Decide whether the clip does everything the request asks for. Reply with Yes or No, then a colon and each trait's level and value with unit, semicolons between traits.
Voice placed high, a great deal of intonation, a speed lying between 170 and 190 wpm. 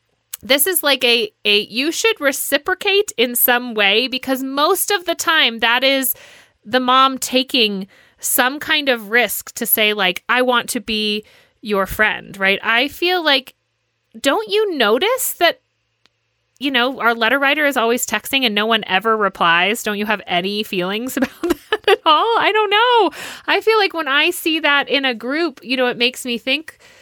Yes: very high, 255 Hz; wide, 6.7 semitones; average, 185 wpm